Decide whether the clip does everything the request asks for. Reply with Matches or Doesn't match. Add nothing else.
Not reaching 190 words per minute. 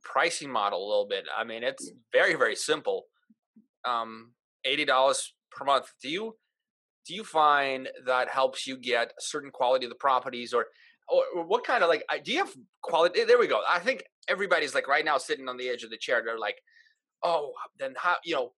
Doesn't match